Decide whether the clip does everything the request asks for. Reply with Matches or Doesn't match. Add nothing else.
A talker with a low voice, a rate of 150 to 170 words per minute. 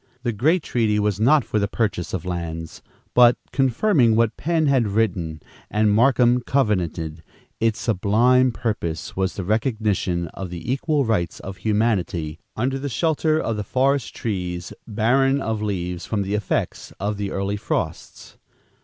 Matches